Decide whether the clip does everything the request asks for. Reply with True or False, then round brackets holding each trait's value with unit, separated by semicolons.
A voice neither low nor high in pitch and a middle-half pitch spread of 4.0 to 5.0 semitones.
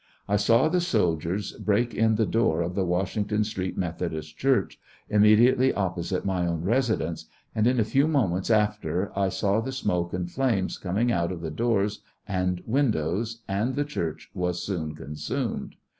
False (100 Hz; 4.5 semitones)